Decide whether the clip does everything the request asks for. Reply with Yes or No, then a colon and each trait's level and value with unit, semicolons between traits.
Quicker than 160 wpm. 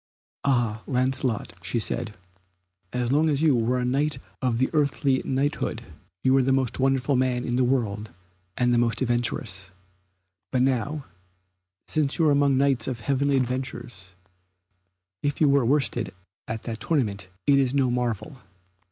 No: average, 155 wpm